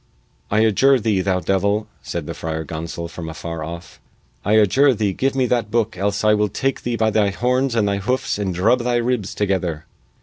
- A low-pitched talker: Yes, low, 105 Hz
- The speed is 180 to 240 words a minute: Yes, average, 200 wpm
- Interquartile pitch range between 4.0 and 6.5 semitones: Yes, average, 4.4 semitones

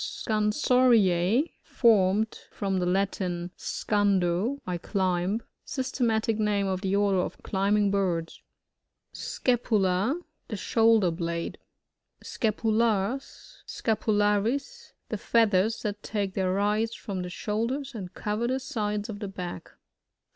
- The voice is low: No, high, 210 Hz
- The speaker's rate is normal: No, slow, 125 wpm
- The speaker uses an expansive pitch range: No, average, 3.2 semitones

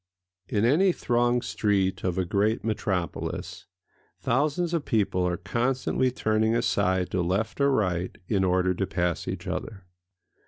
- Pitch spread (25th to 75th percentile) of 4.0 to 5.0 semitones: Yes, average, 4.7 semitones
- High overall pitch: No, low, 105 Hz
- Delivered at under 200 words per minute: Yes, average, 145 wpm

